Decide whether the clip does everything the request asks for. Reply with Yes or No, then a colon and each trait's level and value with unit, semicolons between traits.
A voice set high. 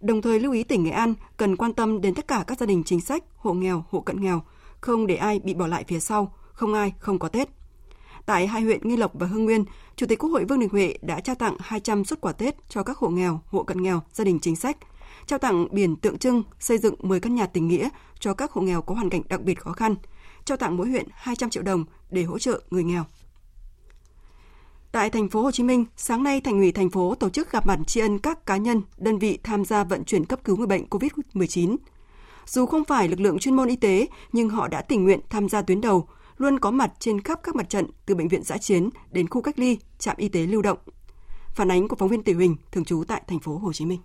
Yes: high, 205 Hz